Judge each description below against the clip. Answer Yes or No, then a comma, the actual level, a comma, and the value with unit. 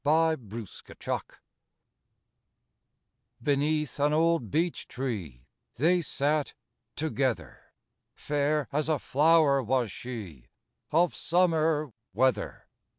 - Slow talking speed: Yes, slow, 95 wpm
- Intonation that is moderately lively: Yes, average, 4.2 semitones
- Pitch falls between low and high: Yes, medium, 145 Hz